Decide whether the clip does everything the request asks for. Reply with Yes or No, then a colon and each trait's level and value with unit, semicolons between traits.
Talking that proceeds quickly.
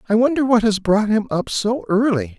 Yes: fast, 225 wpm